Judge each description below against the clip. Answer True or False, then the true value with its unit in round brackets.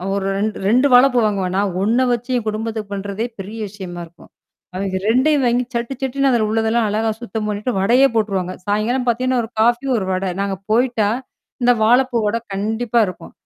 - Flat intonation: False (3.3 semitones)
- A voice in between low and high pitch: False (220 Hz)